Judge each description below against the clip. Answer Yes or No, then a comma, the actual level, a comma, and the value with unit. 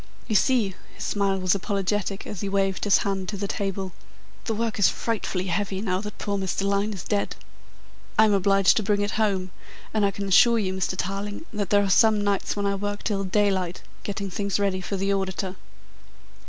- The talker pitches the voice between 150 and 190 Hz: No, high, 200 Hz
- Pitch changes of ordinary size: No, narrow, 1.2 semitones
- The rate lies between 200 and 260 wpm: Yes, fast, 205 wpm